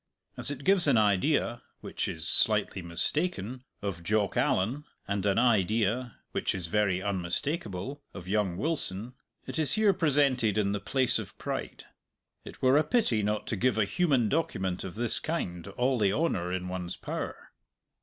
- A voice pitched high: No, low, 110 Hz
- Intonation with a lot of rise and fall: Yes, wide, 6.5 semitones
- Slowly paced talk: No, average, 165 wpm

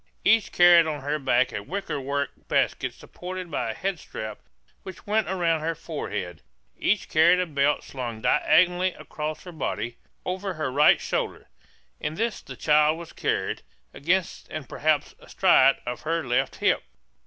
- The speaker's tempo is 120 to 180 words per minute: Yes, average, 155 wpm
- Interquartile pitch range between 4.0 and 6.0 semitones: Yes, average, 4.4 semitones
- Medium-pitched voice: Yes, medium, 155 Hz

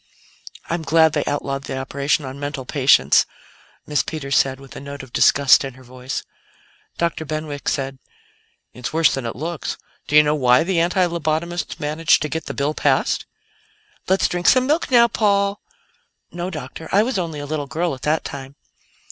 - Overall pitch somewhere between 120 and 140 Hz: No, medium, 150 Hz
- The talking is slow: No, average, 180 wpm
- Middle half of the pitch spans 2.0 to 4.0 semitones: Yes, average, 3.7 semitones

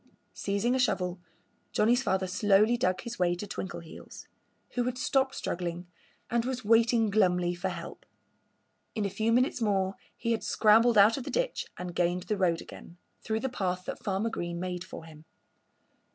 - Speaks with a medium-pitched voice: No, high, 200 Hz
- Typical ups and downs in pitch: Yes, average, 4.4 semitones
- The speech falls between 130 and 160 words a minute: No, average, 175 wpm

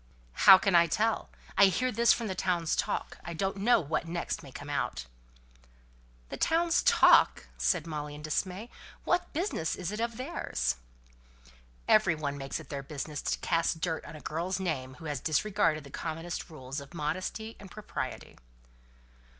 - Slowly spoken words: No, average, 175 wpm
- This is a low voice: No, medium, 170 Hz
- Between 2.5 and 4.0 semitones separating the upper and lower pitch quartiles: No, wide, 5.4 semitones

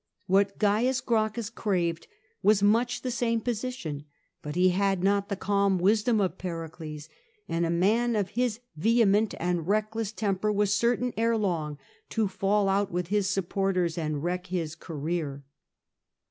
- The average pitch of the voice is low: No, high, 200 Hz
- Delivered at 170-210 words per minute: No, average, 150 wpm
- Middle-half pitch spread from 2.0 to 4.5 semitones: Yes, average, 3.8 semitones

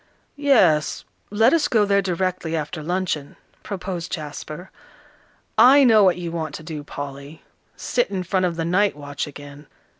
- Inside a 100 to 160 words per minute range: Yes, average, 155 wpm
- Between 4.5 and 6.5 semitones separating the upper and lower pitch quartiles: Yes, average, 4.8 semitones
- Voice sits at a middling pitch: Yes, medium, 175 Hz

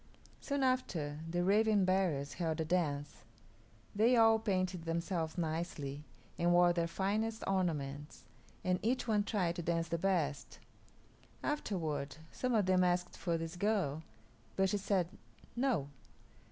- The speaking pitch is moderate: Yes, medium, 180 Hz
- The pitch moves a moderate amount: Yes, average, 4.0 semitones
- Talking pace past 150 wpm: No, average, 140 wpm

